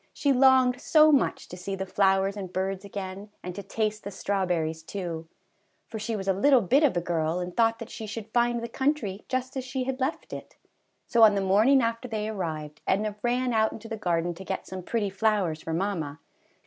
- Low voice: No, high, 205 Hz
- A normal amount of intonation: Yes, average, 4.1 semitones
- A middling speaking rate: No, fast, 215 wpm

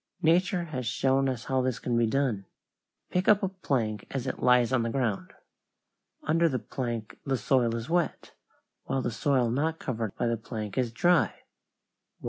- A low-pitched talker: Yes, low, 130 Hz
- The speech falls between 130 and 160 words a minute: No, average, 175 wpm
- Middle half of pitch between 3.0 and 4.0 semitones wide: Yes, average, 3.6 semitones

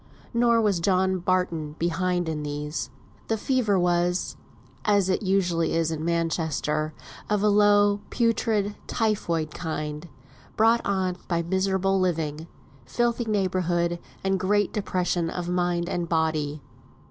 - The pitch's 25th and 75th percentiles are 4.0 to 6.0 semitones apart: No, average, 3.5 semitones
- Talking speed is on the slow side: Yes, slow, 125 wpm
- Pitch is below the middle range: No, medium, 180 Hz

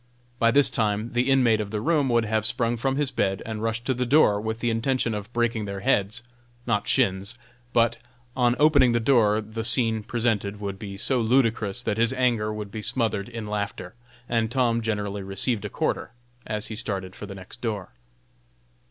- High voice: No, low, 115 Hz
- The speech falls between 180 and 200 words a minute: Yes, average, 195 wpm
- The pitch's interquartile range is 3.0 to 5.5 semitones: No, narrow, 2.6 semitones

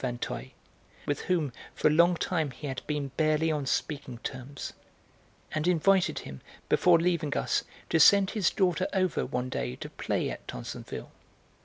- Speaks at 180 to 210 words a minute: No, average, 160 wpm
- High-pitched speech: No, medium, 155 Hz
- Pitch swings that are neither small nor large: Yes, average, 4.6 semitones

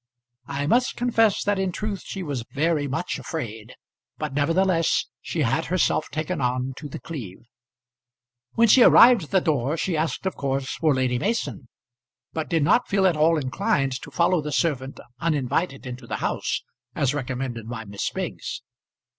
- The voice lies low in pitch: No, medium, 150 Hz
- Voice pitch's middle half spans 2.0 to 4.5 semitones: No, average, 5.3 semitones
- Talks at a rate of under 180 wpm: Yes, average, 170 wpm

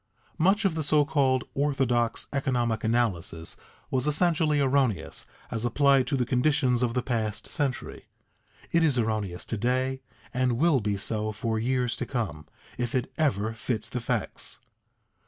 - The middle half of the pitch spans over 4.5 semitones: No, average, 3.8 semitones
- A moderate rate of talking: Yes, average, 155 wpm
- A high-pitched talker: No, low, 125 Hz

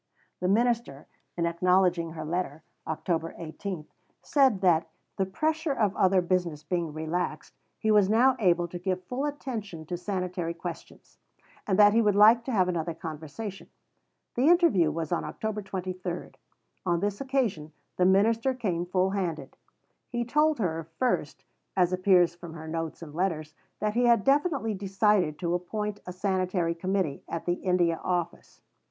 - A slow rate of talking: No, average, 160 wpm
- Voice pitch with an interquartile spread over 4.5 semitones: No, average, 3.9 semitones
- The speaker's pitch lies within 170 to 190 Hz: Yes, medium, 185 Hz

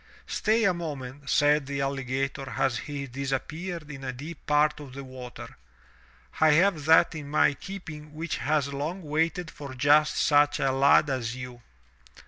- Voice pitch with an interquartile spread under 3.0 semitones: Yes, narrow, 2.5 semitones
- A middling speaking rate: Yes, average, 160 wpm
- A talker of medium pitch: Yes, medium, 145 Hz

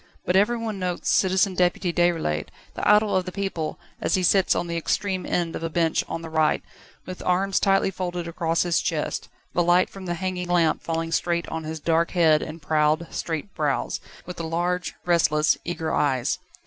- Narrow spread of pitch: Yes, narrow, 2.2 semitones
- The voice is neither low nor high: Yes, medium, 175 Hz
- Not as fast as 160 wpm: No, average, 190 wpm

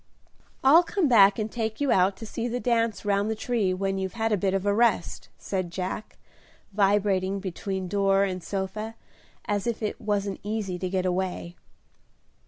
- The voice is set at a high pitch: Yes, high, 200 Hz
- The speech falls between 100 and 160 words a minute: No, average, 180 wpm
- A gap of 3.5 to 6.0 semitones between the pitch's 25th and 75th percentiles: No, average, 2.7 semitones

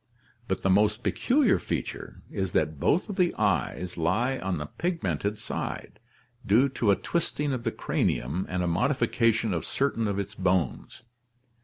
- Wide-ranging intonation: Yes, wide, 6.2 semitones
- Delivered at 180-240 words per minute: No, average, 160 wpm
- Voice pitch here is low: Yes, low, 105 Hz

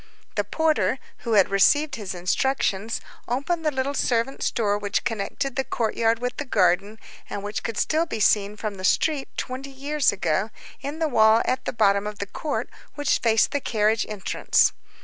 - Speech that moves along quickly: No, average, 180 wpm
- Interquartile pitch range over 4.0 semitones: Yes, average, 4.9 semitones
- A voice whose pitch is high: Yes, high, 230 Hz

